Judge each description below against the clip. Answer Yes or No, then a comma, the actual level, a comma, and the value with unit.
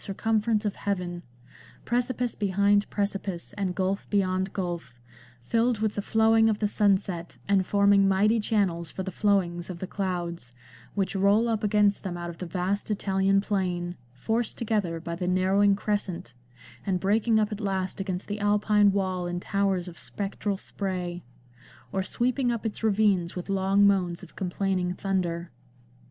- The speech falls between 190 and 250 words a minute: No, average, 160 wpm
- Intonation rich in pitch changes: No, narrow, 2.4 semitones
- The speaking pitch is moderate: No, high, 195 Hz